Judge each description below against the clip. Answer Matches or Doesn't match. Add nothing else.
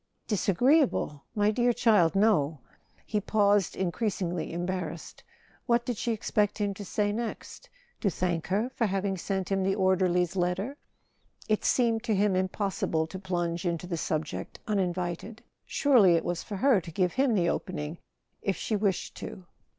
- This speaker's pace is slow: Doesn't match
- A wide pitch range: Doesn't match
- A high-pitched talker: Matches